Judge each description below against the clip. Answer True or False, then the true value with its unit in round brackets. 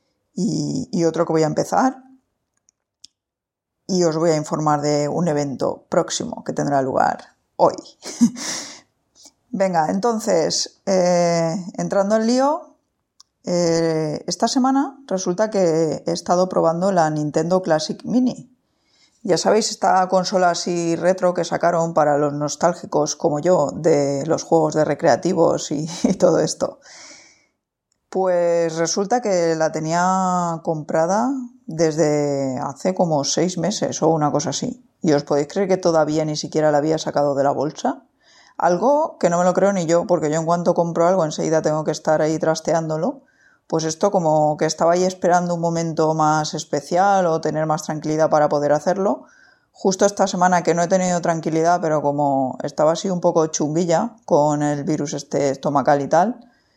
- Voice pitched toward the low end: False (170 Hz)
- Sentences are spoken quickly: False (155 wpm)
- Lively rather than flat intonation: False (3.5 semitones)